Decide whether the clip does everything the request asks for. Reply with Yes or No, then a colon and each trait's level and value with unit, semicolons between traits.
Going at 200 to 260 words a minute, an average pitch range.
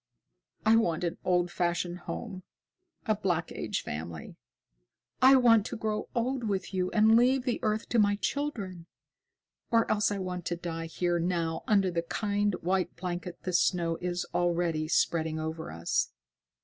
No: average, 160 wpm; average, 4.0 semitones